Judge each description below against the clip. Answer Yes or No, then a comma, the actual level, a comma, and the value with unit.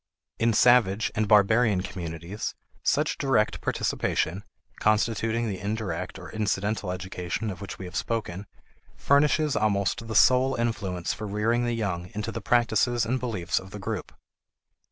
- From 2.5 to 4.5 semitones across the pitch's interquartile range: Yes, average, 3.3 semitones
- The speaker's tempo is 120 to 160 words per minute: Yes, average, 145 wpm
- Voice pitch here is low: Yes, low, 105 Hz